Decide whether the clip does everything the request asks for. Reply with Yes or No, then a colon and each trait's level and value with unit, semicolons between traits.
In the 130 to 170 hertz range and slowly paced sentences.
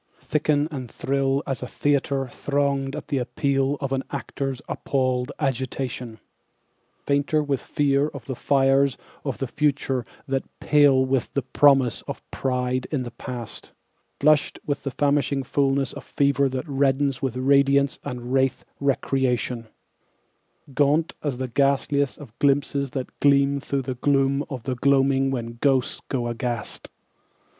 No: low, 135 Hz; average, 145 wpm